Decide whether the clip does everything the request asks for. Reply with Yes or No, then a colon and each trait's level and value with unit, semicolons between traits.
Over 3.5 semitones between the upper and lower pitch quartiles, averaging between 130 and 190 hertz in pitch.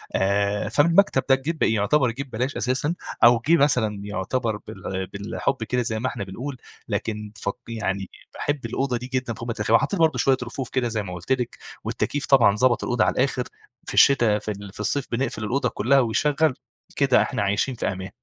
No: average, 4.2 semitones; low, 120 Hz